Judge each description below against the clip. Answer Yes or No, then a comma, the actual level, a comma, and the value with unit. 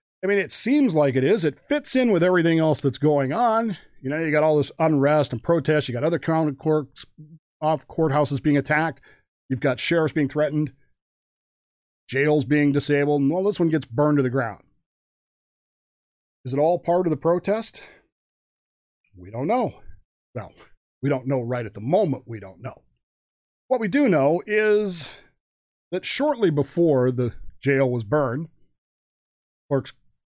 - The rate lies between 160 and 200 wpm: Yes, average, 170 wpm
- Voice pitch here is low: No, medium, 150 Hz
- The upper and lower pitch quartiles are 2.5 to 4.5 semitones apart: Yes, average, 3.8 semitones